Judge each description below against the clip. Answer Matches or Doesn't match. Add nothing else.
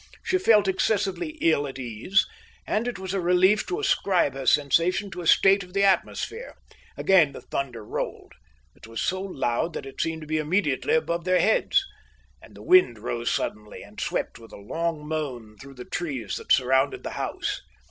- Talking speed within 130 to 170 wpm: Doesn't match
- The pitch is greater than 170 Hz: Doesn't match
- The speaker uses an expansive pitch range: Matches